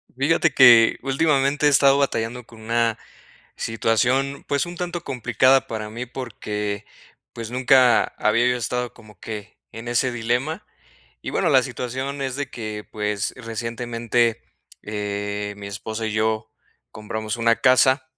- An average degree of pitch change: Yes, average, 3.3 semitones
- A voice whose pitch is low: Yes, low, 120 Hz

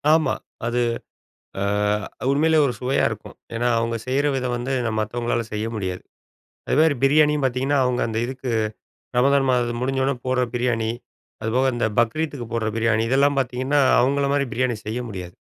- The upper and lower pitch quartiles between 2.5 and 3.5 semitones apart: Yes, average, 2.9 semitones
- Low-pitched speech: Yes, low, 125 Hz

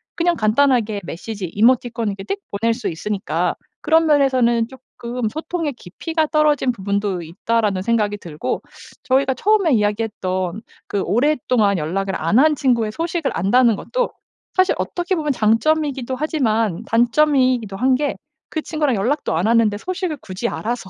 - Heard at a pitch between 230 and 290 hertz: Yes, high, 235 Hz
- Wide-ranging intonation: Yes, wide, 6.1 semitones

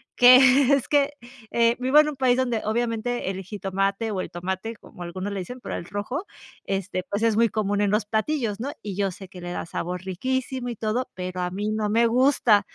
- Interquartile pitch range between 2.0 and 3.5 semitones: No, average, 4.3 semitones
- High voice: Yes, high, 215 Hz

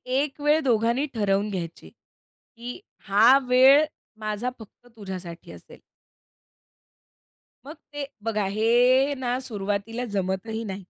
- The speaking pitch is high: Yes, high, 230 Hz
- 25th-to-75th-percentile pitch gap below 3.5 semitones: No, average, 4.2 semitones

